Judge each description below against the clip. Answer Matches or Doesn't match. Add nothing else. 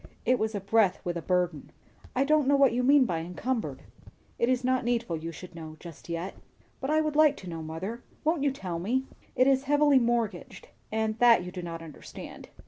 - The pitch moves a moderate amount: Doesn't match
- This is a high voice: Matches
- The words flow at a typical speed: Doesn't match